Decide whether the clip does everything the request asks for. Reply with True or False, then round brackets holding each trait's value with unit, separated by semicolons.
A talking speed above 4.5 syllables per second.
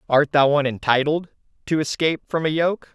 True (5.7 syllables/s)